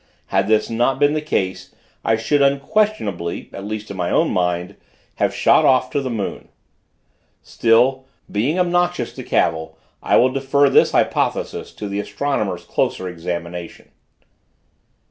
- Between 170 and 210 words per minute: No, average, 145 wpm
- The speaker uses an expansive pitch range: Yes, wide, 6.8 semitones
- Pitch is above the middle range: No, low, 115 Hz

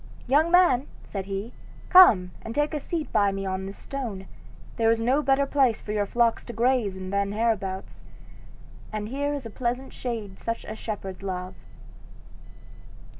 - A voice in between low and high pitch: No, high, 225 Hz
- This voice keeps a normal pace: Yes, average, 170 wpm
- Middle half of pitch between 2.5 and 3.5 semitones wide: No, average, 5.2 semitones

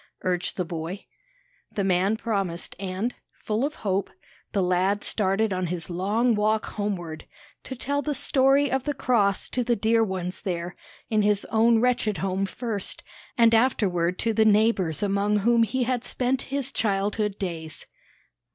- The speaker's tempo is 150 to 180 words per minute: Yes, average, 160 wpm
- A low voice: No, high, 210 Hz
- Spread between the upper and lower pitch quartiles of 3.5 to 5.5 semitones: Yes, average, 3.9 semitones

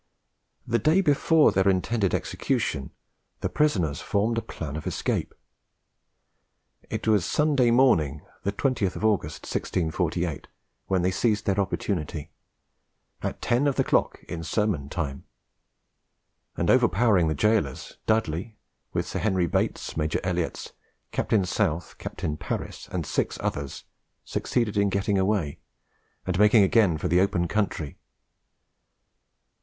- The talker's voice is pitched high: No, very low, 95 Hz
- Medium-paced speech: No, slow, 130 wpm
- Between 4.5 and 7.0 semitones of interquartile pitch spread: Yes, average, 5.1 semitones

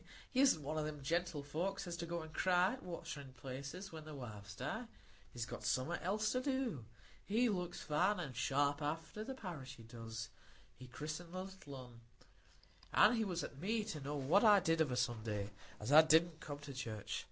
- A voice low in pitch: No, medium, 155 Hz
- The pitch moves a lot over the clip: Yes, wide, 5.8 semitones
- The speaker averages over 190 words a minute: Yes, average, 200 wpm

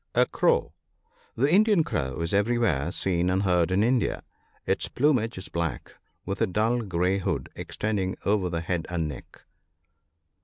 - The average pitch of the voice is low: Yes, very low, 95 Hz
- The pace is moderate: Yes, average, 160 wpm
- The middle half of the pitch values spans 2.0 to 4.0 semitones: No, average, 4.8 semitones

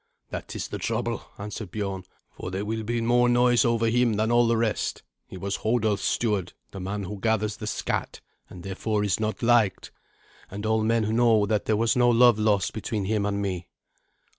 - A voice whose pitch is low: Yes, low, 110 Hz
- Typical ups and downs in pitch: No, narrow, 2.3 semitones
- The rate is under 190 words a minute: No, average, 195 wpm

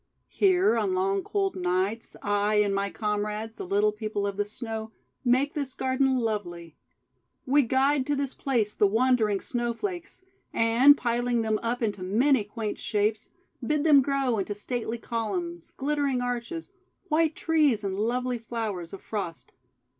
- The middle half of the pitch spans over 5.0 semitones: No, average, 4.5 semitones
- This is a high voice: Yes, high, 230 Hz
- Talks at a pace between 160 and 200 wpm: No, average, 150 wpm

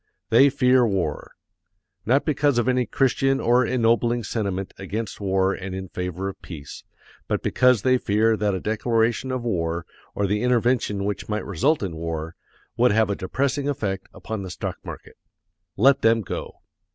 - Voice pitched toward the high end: No, low, 110 Hz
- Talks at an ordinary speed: Yes, average, 165 wpm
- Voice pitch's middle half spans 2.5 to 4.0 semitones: No, average, 4.5 semitones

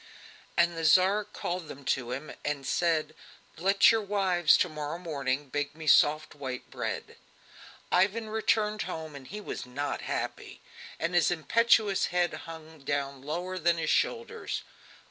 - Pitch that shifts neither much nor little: Yes, average, 4.7 semitones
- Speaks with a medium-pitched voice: Yes, medium, 165 Hz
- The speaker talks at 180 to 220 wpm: No, average, 150 wpm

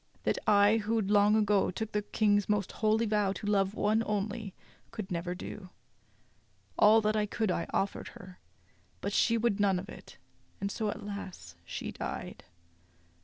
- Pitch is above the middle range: Yes, high, 205 Hz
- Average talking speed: Yes, average, 165 wpm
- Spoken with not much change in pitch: Yes, narrow, 1.6 semitones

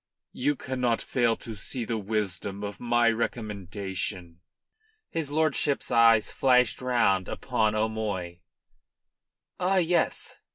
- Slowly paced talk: Yes, slow, 110 wpm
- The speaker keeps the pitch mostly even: No, average, 3.8 semitones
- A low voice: Yes, low, 115 Hz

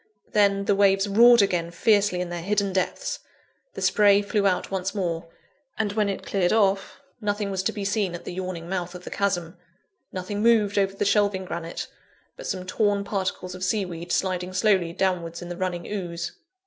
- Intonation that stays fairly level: Yes, narrow, 2.2 semitones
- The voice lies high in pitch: Yes, high, 195 Hz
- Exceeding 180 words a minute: Yes, average, 190 wpm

